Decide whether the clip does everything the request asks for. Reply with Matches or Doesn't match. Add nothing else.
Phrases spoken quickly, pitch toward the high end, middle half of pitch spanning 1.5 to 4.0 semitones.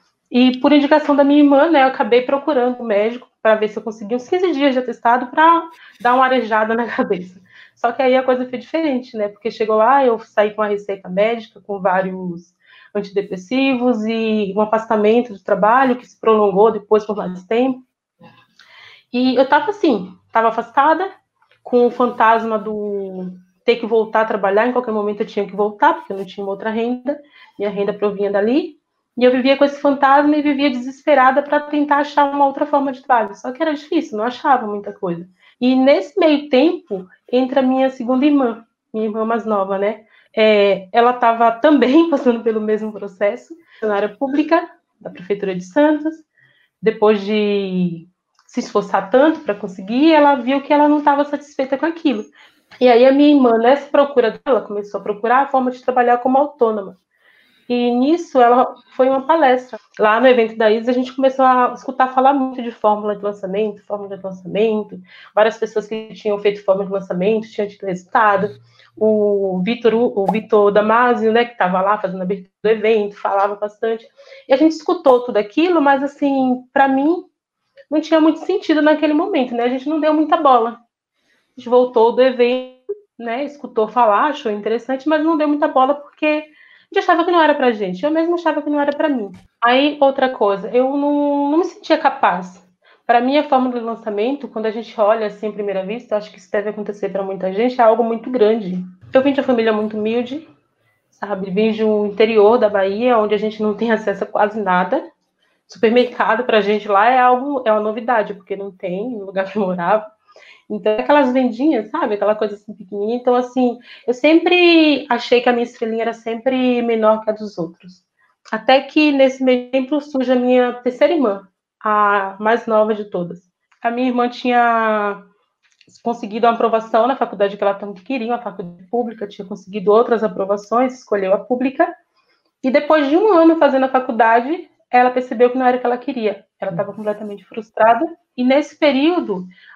Doesn't match